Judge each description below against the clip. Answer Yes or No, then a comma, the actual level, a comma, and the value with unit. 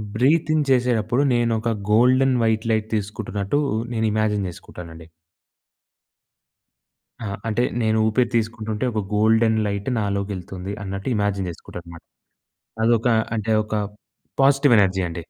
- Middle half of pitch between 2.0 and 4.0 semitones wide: Yes, average, 3.0 semitones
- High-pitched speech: No, low, 110 Hz